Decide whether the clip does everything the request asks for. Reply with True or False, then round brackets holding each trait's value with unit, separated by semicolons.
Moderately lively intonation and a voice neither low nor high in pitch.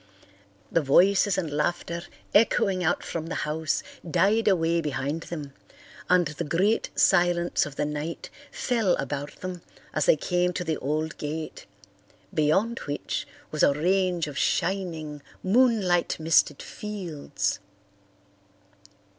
True (3.8 semitones; 170 Hz)